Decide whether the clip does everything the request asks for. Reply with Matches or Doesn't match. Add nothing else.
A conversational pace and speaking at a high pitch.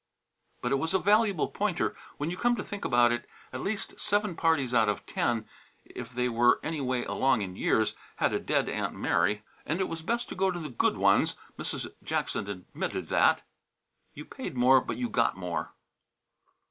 Doesn't match